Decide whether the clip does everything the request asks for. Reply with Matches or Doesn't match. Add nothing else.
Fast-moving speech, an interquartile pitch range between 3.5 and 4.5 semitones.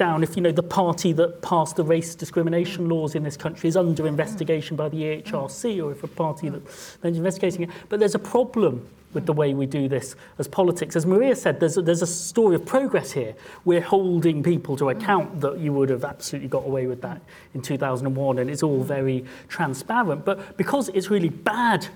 Matches